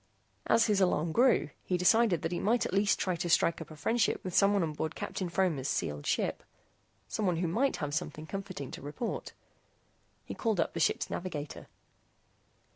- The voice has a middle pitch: Yes, medium, 180 Hz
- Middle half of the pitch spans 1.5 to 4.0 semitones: No, average, 4.4 semitones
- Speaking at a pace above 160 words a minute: Yes, average, 185 wpm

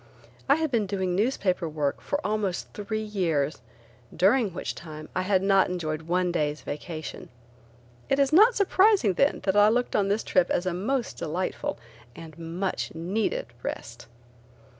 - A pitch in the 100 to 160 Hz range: No, high, 190 Hz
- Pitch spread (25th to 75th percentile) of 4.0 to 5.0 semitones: Yes, average, 4.6 semitones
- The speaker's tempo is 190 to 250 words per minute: No, average, 160 wpm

